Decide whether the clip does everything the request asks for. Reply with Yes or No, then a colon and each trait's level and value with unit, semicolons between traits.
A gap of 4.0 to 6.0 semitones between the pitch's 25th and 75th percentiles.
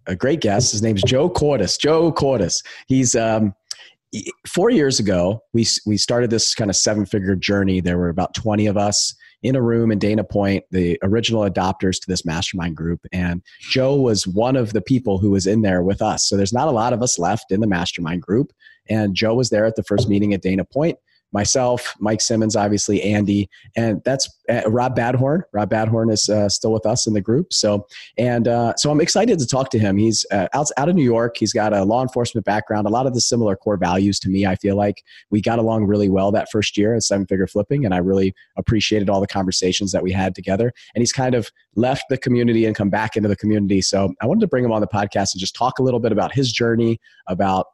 No: average, 3.1 semitones